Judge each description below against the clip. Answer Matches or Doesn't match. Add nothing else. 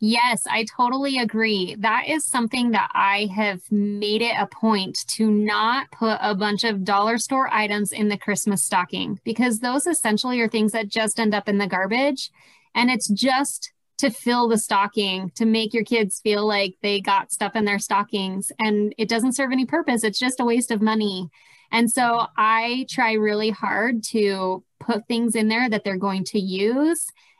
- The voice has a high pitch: Matches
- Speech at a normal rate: Matches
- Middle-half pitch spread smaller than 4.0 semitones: Matches